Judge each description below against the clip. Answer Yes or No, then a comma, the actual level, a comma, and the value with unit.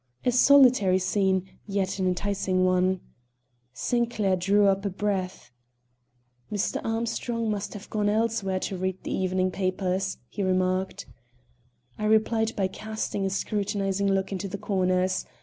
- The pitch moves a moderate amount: No, narrow, 2.1 semitones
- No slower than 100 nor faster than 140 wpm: Yes, slow, 135 wpm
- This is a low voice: No, high, 195 Hz